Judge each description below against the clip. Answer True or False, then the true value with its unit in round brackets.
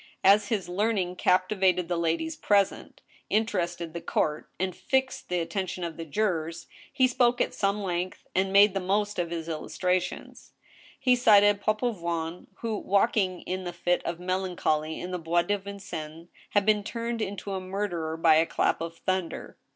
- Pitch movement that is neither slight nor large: True (3.2 semitones)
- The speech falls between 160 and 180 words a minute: True (165 wpm)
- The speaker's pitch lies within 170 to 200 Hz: True (185 Hz)